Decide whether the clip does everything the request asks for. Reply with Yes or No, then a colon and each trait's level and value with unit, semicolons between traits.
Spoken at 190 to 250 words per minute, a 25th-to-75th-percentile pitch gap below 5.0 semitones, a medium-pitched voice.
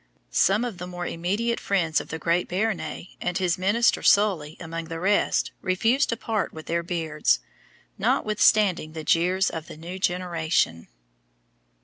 No: average, 150 wpm; average, 3.5 semitones; medium, 180 Hz